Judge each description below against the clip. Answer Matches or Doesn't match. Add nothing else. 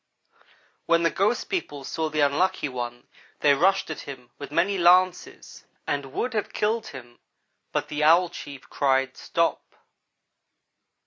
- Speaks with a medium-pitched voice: Matches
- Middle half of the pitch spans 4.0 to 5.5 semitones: Matches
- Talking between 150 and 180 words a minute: Doesn't match